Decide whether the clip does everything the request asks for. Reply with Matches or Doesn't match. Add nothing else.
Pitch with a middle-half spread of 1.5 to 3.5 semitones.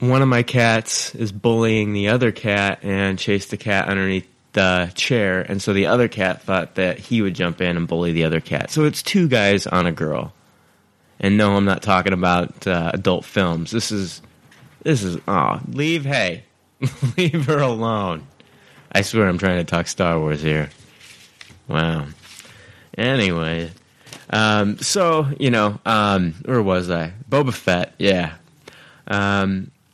Doesn't match